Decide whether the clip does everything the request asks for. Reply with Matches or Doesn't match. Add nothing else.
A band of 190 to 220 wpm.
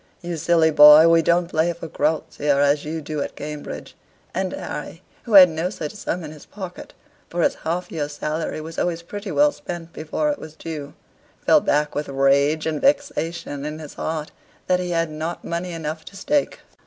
Matches